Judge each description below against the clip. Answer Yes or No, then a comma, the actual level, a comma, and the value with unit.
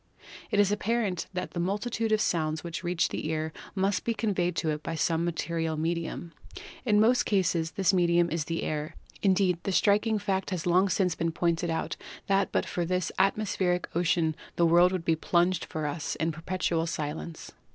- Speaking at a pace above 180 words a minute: Yes, average, 190 wpm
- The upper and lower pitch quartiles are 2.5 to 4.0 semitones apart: Yes, average, 2.9 semitones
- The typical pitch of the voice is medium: Yes, medium, 175 Hz